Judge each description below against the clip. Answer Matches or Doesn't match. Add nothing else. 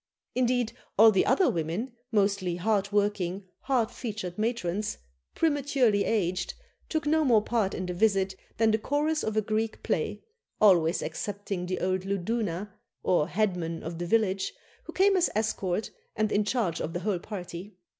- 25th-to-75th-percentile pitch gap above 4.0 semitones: Doesn't match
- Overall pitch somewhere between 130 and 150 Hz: Doesn't match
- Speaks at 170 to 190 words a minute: Doesn't match